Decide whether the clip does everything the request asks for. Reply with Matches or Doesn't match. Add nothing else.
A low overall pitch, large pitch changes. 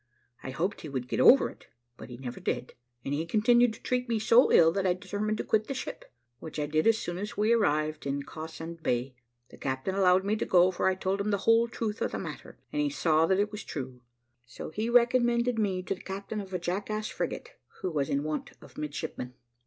Doesn't match